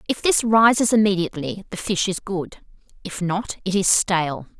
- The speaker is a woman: Yes, female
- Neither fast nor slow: Yes, average, 170 wpm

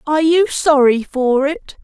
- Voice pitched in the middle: No, very high, 290 Hz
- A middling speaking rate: Yes, average, 165 wpm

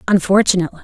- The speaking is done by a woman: Yes, female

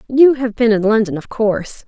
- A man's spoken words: No, female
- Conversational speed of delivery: No, fast, 225 wpm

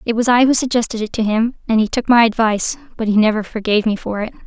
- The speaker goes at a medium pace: No, fast, 270 wpm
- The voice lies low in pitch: No, high, 225 Hz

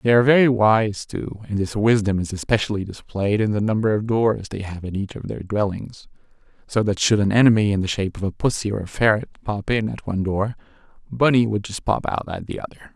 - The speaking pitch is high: No, low, 105 Hz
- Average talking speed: No, fast, 230 wpm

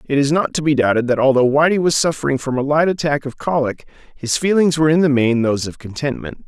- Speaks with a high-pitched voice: No, medium, 145 Hz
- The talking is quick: Yes, fast, 240 wpm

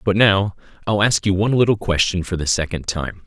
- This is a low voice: Yes, low, 100 Hz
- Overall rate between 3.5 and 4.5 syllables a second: No, 5.6 syllables/s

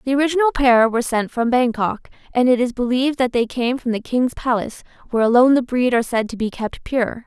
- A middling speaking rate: No, fast, 230 wpm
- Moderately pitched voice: No, high, 245 Hz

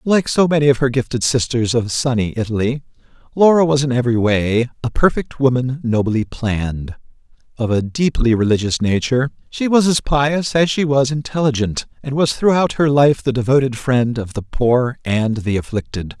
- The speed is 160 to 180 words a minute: Yes, average, 175 wpm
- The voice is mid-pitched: No, low, 130 Hz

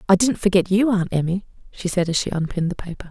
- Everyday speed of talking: No, fast, 250 wpm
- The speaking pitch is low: No, medium, 185 Hz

